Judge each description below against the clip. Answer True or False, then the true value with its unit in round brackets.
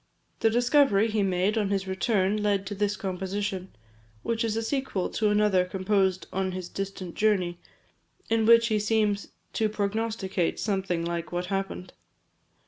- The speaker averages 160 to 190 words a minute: False (150 wpm)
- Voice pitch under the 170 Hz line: False (200 Hz)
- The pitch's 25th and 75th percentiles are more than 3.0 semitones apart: False (2.4 semitones)